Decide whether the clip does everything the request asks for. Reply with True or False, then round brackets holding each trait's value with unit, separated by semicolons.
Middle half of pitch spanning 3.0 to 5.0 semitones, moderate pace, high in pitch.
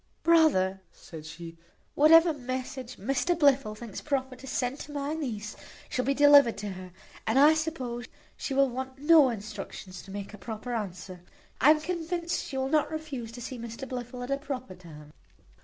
False (5.4 semitones; 180 wpm; 255 Hz)